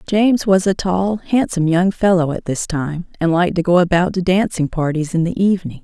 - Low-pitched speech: No, medium, 180 Hz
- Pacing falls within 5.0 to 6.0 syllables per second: Yes, 5.6 syllables/s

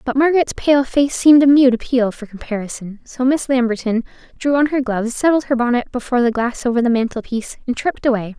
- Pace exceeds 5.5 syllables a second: Yes, 6.2 syllables/s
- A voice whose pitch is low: No, very high, 250 Hz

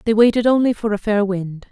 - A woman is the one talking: Yes, female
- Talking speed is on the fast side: Yes, fast, 245 wpm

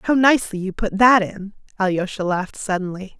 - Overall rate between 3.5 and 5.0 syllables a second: No, 5.5 syllables/s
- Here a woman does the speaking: Yes, female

